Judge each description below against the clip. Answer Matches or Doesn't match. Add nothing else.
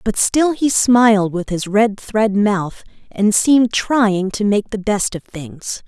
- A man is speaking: Doesn't match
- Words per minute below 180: Doesn't match